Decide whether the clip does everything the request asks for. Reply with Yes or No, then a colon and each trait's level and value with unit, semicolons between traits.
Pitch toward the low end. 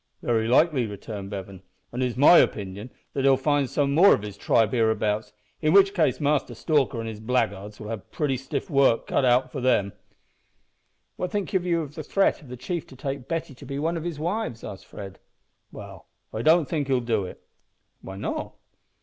Yes: low, 130 Hz